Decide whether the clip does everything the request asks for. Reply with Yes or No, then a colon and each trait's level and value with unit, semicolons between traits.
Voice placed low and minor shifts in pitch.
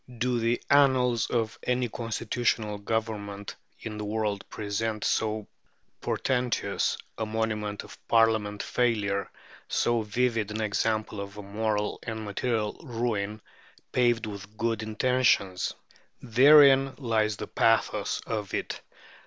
Yes: low, 110 Hz; narrow, 2.3 semitones